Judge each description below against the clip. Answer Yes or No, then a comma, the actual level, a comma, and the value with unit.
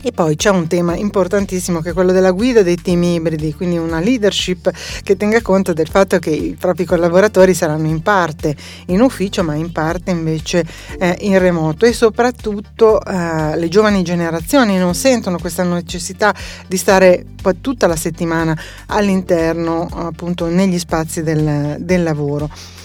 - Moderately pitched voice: Yes, medium, 180 Hz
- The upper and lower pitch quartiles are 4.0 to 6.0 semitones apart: No, average, 2.8 semitones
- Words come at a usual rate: Yes, average, 160 wpm